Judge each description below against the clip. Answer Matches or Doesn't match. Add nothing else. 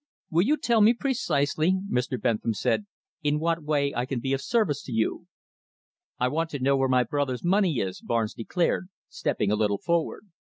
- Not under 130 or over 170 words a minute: Doesn't match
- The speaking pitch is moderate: Matches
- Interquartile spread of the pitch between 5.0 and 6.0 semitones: Matches